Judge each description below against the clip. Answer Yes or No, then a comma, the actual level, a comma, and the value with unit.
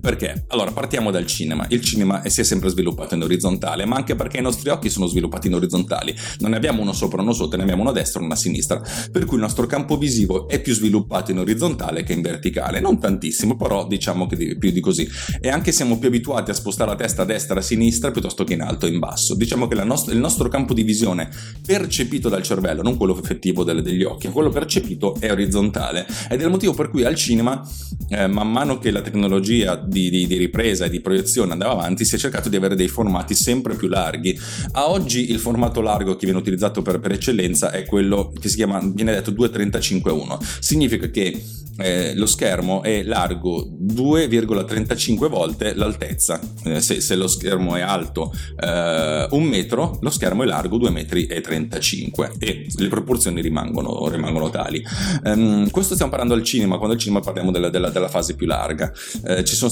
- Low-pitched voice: Yes, low, 105 Hz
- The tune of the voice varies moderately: Yes, average, 4.1 semitones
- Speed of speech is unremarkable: No, fast, 205 wpm